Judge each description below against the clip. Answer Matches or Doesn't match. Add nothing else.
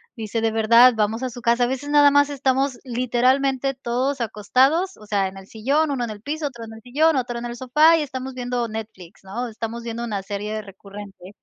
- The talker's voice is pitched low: Doesn't match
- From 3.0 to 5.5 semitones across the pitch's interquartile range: Matches